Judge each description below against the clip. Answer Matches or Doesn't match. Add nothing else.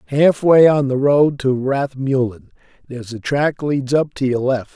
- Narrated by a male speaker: Matches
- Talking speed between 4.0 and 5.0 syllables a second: Matches